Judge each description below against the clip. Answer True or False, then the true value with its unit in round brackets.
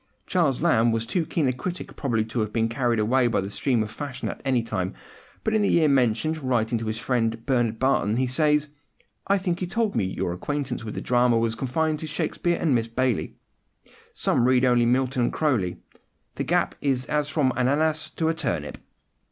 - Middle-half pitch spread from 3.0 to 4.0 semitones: False (4.7 semitones)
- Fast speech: True (210 wpm)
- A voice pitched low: True (130 Hz)